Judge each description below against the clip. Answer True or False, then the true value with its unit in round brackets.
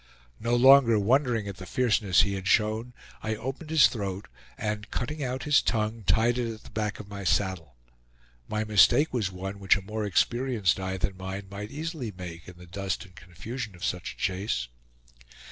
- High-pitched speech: False (105 Hz)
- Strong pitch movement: False (4.0 semitones)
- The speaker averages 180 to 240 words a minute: True (190 wpm)